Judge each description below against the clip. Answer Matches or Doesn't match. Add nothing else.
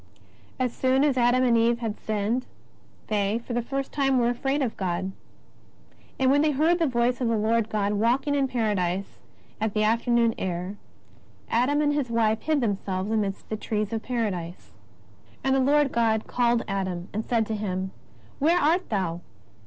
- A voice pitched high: Matches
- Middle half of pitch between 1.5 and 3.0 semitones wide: Doesn't match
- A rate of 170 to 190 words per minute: Matches